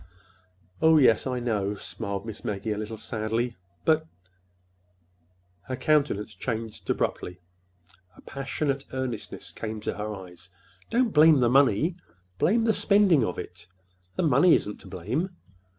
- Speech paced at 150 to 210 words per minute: No, slow, 135 wpm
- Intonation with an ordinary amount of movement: No, wide, 6.7 semitones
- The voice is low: Yes, low, 120 Hz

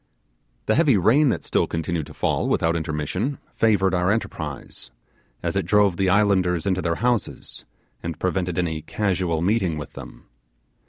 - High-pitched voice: No, very low, 95 Hz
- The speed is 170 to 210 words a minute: No, average, 155 wpm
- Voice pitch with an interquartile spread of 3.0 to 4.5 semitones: Yes, average, 3.9 semitones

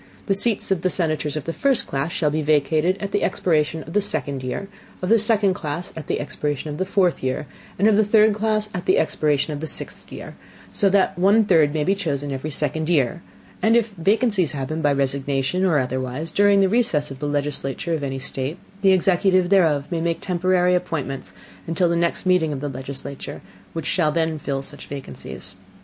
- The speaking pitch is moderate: Yes, medium, 160 Hz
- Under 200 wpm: No, fast, 205 wpm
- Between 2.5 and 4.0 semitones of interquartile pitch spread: No, average, 4.8 semitones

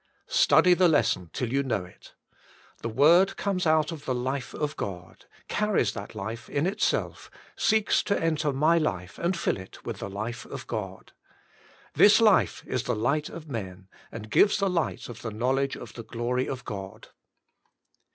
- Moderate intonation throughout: No, wide, 7.2 semitones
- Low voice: Yes, low, 130 Hz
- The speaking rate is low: No, average, 175 wpm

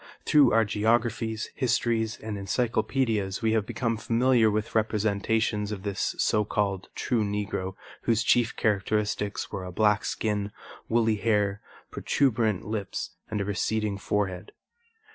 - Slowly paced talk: Yes, slow, 130 wpm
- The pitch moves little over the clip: Yes, narrow, 1.8 semitones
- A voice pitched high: No, low, 110 Hz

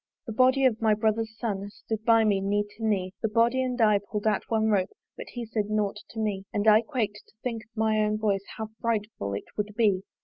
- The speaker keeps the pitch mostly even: Yes, narrow, 1.7 semitones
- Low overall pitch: No, high, 215 Hz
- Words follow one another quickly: Yes, fast, 235 wpm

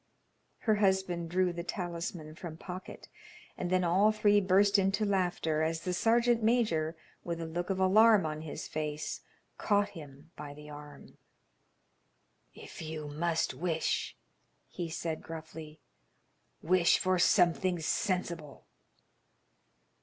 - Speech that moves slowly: Yes, slow, 125 wpm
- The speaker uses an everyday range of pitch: Yes, average, 3.2 semitones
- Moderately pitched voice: Yes, medium, 175 Hz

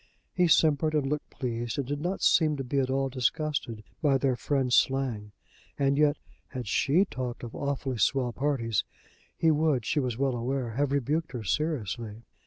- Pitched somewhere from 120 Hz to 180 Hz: Yes, low, 135 Hz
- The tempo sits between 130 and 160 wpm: No, average, 180 wpm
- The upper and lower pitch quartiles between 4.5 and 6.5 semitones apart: No, average, 3.3 semitones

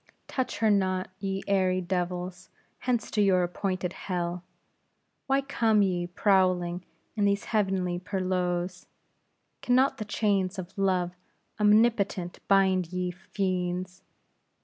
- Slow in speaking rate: Yes, slow, 120 wpm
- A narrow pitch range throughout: Yes, narrow, 2.1 semitones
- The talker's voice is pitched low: No, medium, 185 Hz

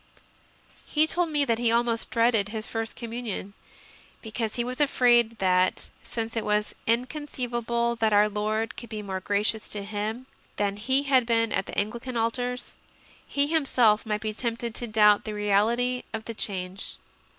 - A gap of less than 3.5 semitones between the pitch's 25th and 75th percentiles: Yes, narrow, 2.5 semitones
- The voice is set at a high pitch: Yes, high, 225 Hz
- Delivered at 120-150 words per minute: No, average, 170 wpm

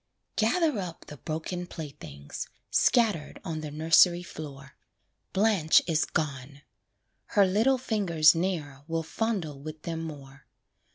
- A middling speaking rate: No, slow, 120 wpm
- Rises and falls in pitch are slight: No, average, 4.4 semitones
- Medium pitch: Yes, medium, 160 Hz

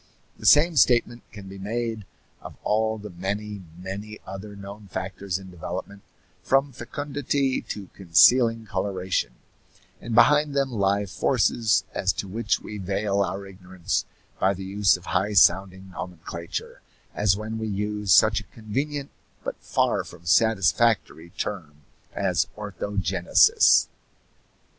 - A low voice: Yes, low, 100 Hz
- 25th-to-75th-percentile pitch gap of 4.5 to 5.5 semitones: No, average, 3.0 semitones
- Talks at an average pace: No, slow, 130 wpm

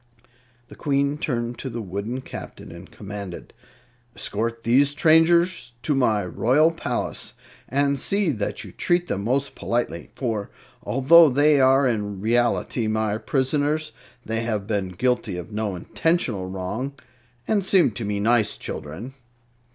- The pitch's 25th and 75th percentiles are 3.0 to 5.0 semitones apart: No, wide, 5.4 semitones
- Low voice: Yes, low, 120 Hz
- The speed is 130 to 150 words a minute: Yes, average, 140 wpm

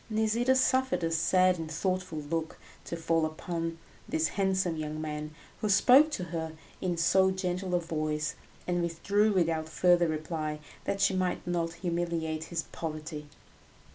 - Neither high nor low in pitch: Yes, medium, 170 Hz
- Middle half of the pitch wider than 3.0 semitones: No, average, 2.7 semitones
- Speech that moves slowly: No, average, 150 wpm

